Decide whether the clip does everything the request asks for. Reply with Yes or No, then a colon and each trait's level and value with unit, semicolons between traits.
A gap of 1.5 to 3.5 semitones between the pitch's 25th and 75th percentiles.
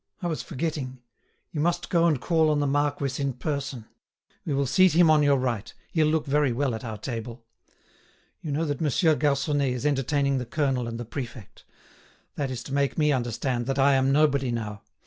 Yes: average, 3.0 semitones